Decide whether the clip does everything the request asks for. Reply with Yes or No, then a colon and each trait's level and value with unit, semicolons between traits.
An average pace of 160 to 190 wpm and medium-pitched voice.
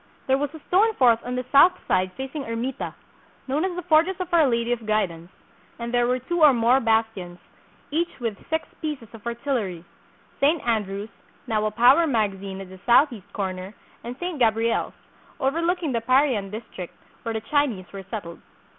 No: average, 180 wpm; high, 240 Hz